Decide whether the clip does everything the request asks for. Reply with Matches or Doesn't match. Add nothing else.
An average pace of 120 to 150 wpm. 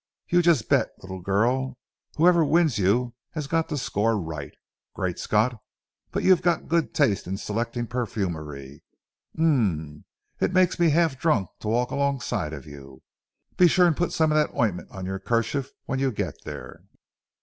Doesn't match